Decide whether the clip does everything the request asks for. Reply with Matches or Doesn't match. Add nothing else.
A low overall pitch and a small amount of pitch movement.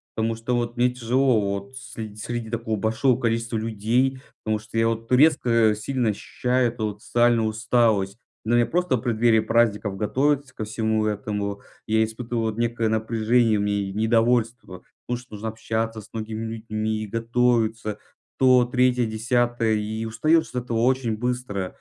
Matches